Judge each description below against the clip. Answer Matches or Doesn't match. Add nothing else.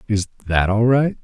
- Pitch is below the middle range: Matches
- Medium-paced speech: Matches